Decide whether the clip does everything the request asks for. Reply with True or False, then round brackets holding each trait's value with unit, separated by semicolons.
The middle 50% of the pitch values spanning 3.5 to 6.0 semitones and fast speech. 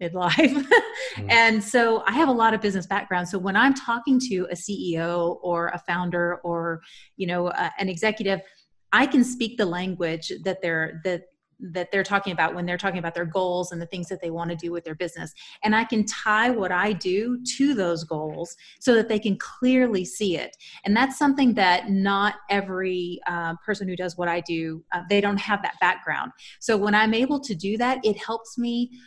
True (4.3 semitones; 210 wpm)